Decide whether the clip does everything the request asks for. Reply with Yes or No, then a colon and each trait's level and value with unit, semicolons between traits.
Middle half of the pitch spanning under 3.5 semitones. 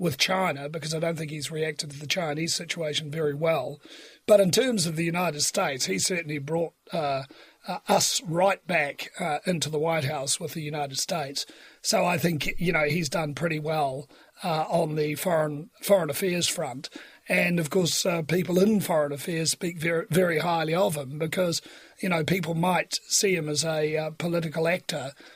Yes: average, 2.7 semitones